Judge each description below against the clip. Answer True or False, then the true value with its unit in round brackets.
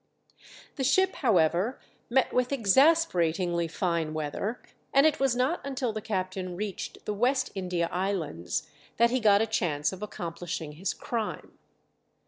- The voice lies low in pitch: False (200 Hz)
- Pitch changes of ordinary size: False (6.5 semitones)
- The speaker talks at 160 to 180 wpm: False (140 wpm)